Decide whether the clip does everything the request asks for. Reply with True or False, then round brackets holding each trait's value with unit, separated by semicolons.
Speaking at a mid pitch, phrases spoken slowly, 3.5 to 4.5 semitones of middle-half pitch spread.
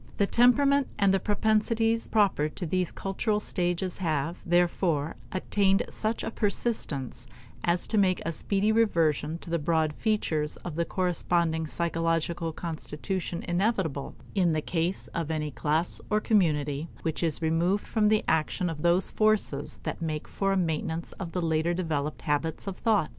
False (175 Hz; 160 wpm; 3.9 semitones)